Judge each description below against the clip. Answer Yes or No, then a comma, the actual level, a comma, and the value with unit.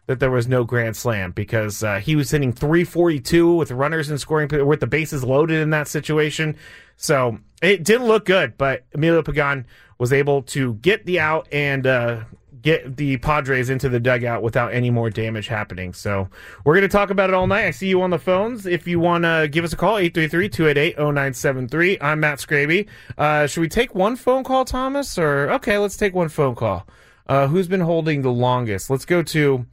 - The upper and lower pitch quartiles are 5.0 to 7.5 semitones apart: Yes, average, 5.3 semitones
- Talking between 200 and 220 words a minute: Yes, fast, 205 wpm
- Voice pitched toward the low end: No, medium, 150 Hz